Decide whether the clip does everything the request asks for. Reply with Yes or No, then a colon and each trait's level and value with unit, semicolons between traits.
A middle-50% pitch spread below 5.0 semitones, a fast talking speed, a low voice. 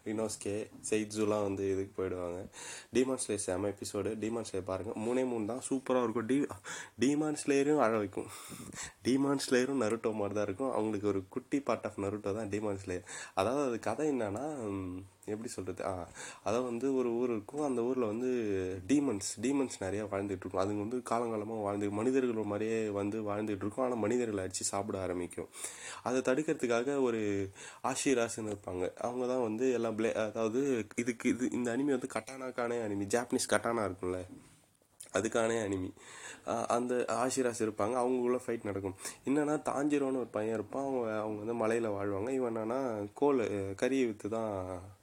Yes: average, 3.8 semitones; fast, 150 wpm; low, 110 Hz